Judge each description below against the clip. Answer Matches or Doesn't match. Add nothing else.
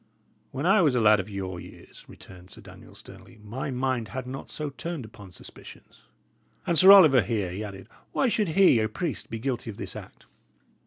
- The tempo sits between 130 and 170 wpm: Doesn't match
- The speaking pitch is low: Matches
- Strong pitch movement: Matches